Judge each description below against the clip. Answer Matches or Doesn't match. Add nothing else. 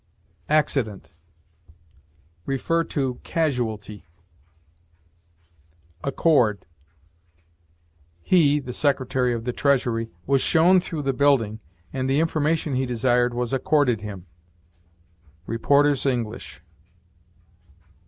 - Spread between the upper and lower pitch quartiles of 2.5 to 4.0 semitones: Matches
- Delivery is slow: Matches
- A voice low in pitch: Matches